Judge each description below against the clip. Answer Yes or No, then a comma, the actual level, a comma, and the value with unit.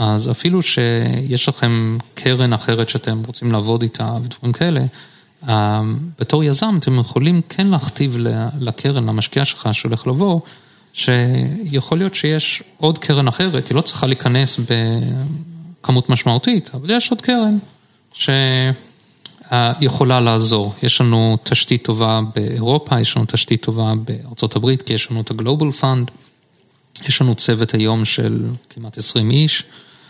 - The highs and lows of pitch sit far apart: No, average, 4.1 semitones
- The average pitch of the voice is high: No, low, 125 Hz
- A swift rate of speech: No, average, 130 wpm